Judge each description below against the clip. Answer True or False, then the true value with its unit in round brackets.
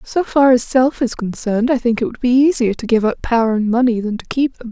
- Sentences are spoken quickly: True (280 wpm)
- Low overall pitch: False (240 Hz)